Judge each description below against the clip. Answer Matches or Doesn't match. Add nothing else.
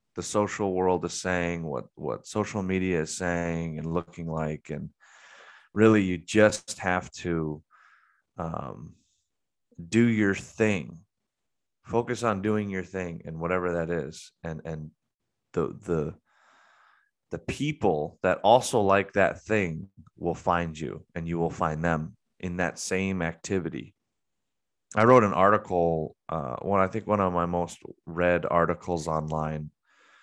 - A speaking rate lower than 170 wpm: Matches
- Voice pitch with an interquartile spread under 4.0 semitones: Matches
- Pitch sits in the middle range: Doesn't match